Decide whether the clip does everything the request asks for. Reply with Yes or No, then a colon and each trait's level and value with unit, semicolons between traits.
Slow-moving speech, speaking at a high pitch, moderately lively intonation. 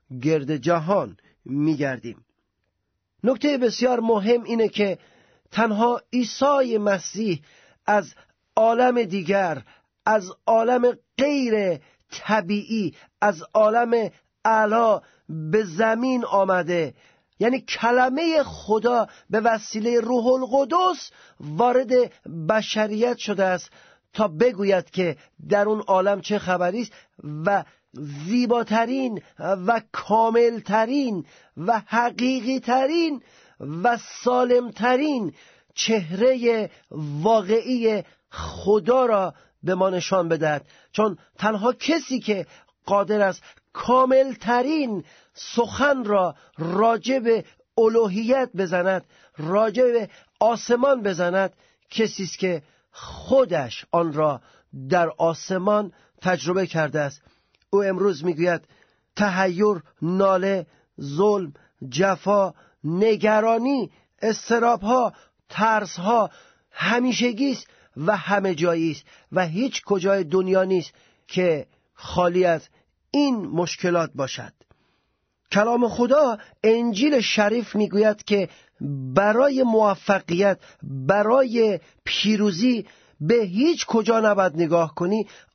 Yes: slow, 95 wpm; high, 210 Hz; average, 4.9 semitones